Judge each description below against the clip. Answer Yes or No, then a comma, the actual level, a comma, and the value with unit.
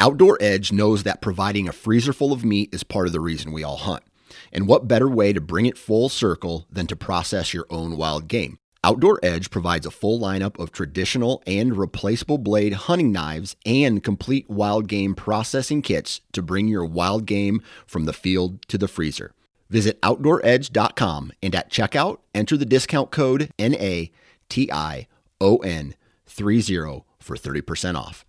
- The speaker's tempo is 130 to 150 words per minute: No, average, 175 wpm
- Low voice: Yes, low, 100 Hz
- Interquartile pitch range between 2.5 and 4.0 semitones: No, average, 5.1 semitones